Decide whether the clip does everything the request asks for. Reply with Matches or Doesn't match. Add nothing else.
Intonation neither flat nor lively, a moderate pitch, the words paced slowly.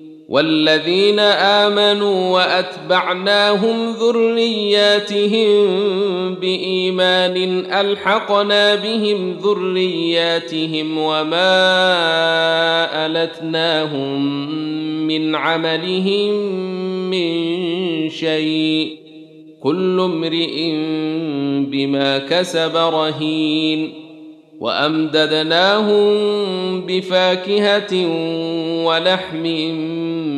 Matches